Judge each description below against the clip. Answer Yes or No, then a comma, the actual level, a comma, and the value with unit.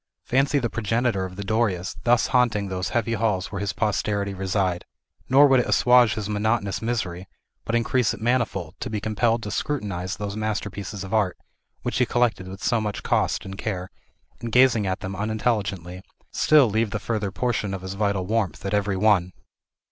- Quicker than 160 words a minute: Yes, average, 185 wpm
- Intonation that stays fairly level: No, average, 3.2 semitones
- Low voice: Yes, low, 105 Hz